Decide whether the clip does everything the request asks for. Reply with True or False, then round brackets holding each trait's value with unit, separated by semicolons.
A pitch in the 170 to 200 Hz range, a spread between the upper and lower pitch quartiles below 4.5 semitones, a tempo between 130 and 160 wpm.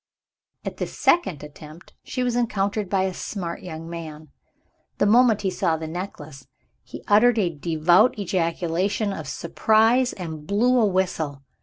False (185 Hz; 4.9 semitones; 150 wpm)